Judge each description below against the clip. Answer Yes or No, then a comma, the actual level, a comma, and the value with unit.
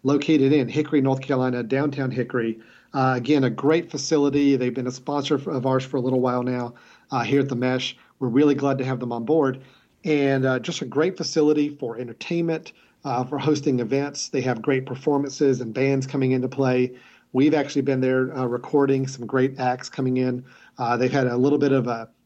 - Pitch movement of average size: No, narrow, 2.2 semitones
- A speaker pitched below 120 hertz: No, low, 135 Hz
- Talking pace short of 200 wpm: No, fast, 205 wpm